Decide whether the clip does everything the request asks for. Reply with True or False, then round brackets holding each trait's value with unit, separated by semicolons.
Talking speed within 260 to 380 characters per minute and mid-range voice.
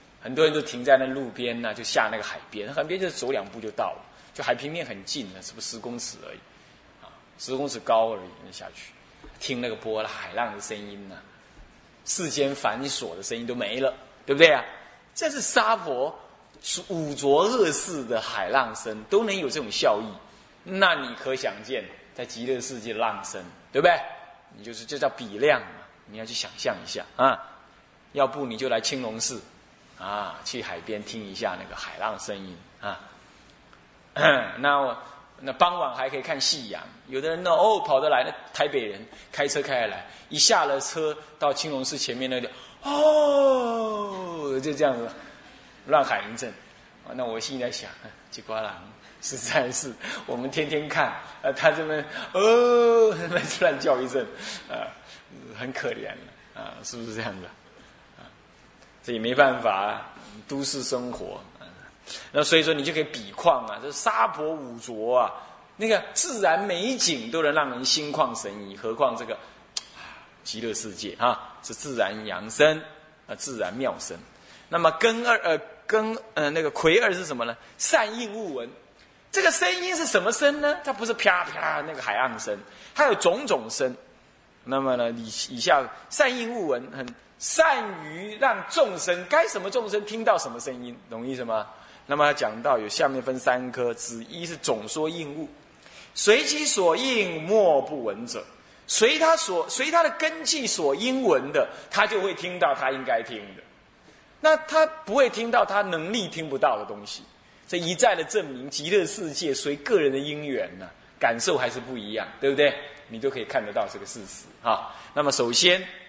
False (250 characters per minute; 155 Hz)